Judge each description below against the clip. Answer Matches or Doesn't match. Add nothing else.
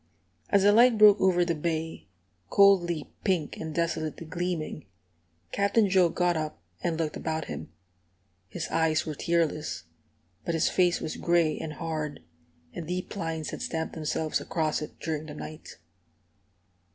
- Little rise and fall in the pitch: Matches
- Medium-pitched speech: Matches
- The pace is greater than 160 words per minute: Doesn't match